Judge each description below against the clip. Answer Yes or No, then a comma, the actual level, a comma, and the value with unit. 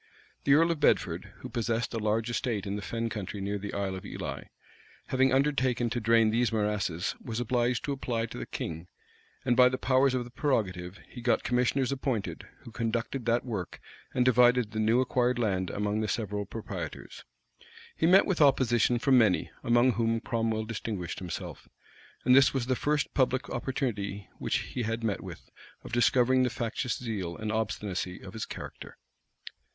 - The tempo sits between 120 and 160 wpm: No, average, 180 wpm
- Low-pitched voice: Yes, low, 115 Hz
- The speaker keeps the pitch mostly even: No, average, 3.1 semitones